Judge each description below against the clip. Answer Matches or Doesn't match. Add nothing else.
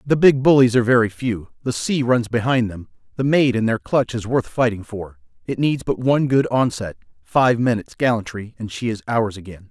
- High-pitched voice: Doesn't match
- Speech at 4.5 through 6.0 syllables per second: Matches